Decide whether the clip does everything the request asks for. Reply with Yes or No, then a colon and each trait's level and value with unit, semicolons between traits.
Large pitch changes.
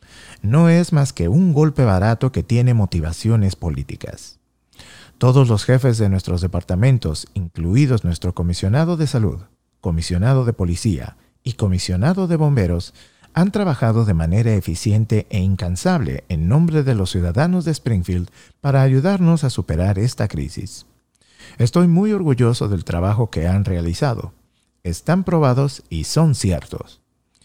Yes: wide, 7.3 semitones